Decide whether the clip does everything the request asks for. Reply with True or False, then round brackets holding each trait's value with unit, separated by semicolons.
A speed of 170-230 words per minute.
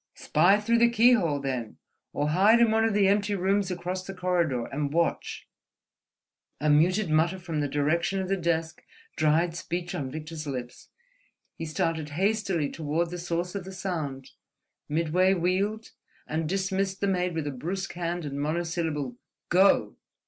False (155 wpm)